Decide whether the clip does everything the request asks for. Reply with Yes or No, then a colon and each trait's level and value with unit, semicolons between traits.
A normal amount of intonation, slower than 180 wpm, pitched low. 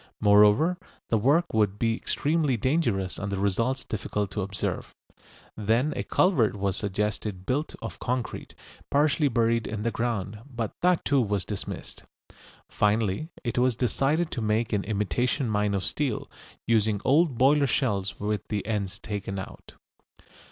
Yes: average, 4.2 semitones; average, 150 wpm; low, 110 Hz